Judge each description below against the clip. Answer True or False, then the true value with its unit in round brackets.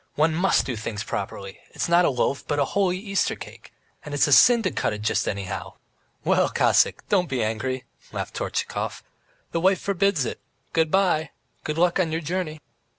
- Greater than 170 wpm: True (190 wpm)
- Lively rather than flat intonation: True (6.6 semitones)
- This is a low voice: False (155 Hz)